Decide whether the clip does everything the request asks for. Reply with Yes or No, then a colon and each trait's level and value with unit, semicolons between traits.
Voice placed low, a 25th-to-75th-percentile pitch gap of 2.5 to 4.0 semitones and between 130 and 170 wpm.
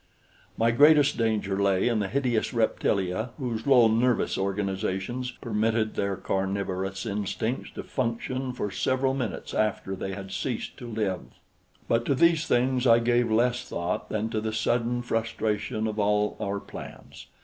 Yes: low, 110 Hz; average, 3.4 semitones; average, 150 wpm